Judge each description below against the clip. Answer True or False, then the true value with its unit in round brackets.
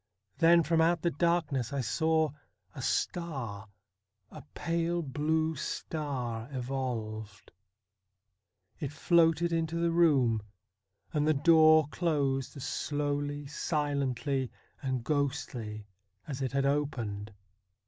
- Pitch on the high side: False (145 Hz)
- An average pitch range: True (4.0 semitones)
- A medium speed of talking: False (115 wpm)